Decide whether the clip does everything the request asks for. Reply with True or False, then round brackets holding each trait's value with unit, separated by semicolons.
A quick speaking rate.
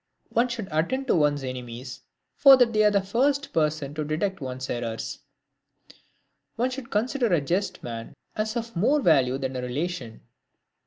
False (160 wpm)